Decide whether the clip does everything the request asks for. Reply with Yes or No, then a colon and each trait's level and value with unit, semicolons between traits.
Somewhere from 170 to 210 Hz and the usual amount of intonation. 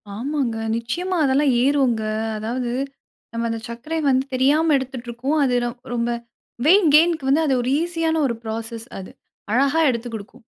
No: very high, 260 Hz; average, 4.5 semitones